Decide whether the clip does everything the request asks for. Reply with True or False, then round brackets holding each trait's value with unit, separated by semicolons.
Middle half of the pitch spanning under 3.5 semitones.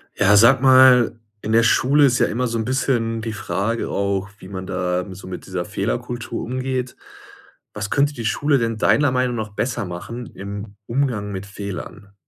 False (4.0 semitones)